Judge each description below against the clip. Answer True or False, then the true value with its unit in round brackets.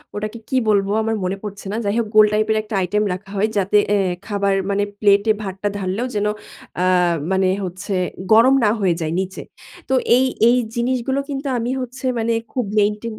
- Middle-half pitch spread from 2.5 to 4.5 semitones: True (2.9 semitones)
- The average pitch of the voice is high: True (210 Hz)